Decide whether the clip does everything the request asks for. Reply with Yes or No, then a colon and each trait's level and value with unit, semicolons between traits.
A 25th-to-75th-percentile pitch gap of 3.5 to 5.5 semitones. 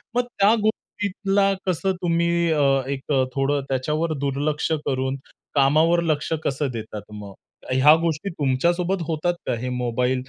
Yes: average, 4.5 semitones